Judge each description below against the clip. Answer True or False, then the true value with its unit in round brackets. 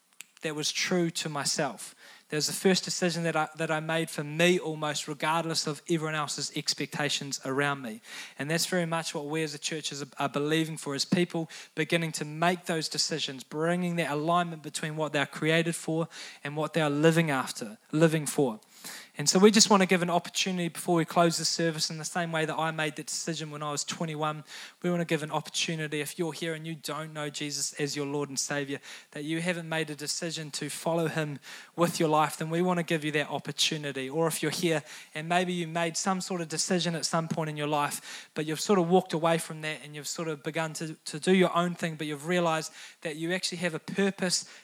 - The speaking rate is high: True (235 wpm)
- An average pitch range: False (2.2 semitones)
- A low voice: False (160 Hz)